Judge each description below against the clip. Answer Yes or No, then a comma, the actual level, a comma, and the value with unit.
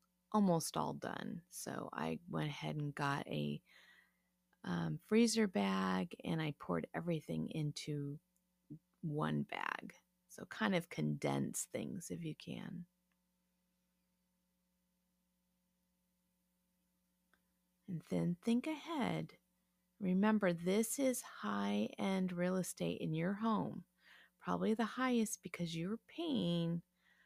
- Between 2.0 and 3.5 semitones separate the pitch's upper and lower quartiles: Yes, average, 2.7 semitones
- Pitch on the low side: No, medium, 180 Hz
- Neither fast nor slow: No, slow, 105 wpm